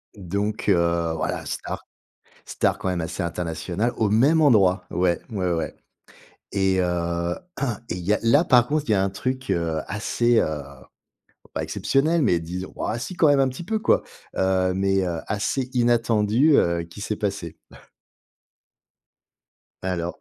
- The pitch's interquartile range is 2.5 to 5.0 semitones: No, wide, 5.5 semitones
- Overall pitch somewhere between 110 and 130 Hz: No, low, 100 Hz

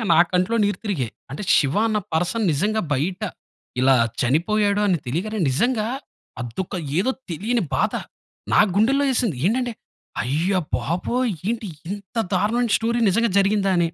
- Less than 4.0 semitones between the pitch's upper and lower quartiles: No, average, 5.0 semitones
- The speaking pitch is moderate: No, high, 200 Hz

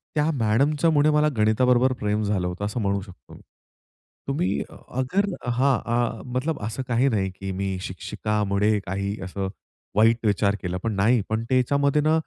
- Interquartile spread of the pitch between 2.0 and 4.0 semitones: No, average, 4.7 semitones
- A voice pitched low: Yes, low, 110 Hz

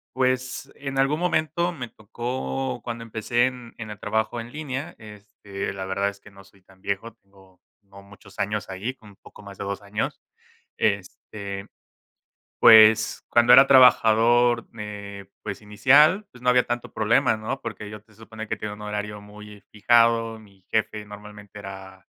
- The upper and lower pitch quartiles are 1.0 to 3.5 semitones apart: Yes, average, 3.1 semitones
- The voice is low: Yes, low, 110 Hz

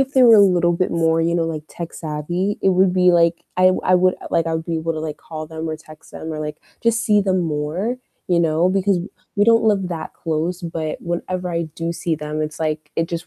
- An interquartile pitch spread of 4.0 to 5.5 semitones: No, narrow, 2.5 semitones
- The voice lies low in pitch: No, medium, 170 Hz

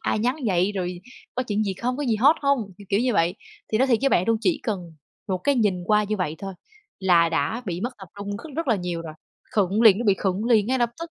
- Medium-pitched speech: No, high, 210 Hz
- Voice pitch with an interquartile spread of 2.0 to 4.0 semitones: No, average, 4.8 semitones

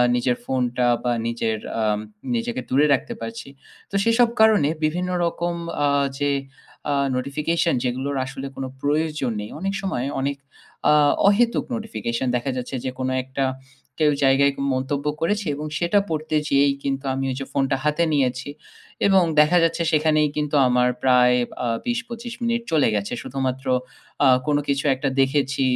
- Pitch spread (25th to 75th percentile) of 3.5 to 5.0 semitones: Yes, average, 4.3 semitones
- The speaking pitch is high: No, medium, 140 Hz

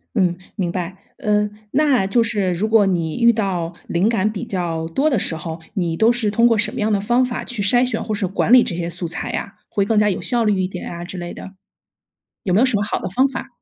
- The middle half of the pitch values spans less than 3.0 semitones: No, average, 4.6 semitones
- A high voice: Yes, high, 205 Hz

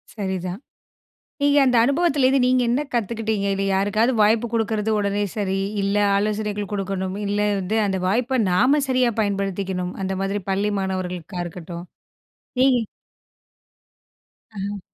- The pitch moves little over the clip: No, average, 3.4 semitones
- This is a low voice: No, high, 205 Hz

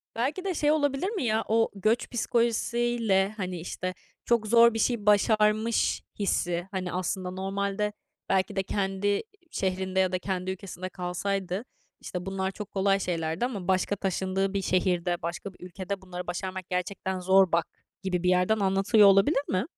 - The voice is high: Yes, high, 195 Hz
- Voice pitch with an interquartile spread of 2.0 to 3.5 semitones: Yes, average, 2.7 semitones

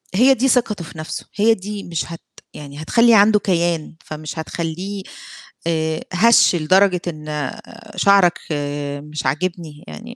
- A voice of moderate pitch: Yes, medium, 175 Hz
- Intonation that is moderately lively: Yes, average, 4.5 semitones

